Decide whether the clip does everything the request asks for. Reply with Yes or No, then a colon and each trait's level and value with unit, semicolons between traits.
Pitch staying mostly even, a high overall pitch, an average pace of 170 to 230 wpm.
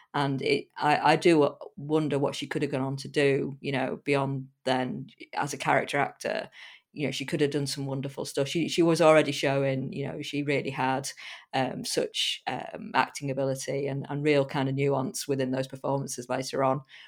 No: narrow, 1.4 semitones; medium, 140 Hz; average, 200 wpm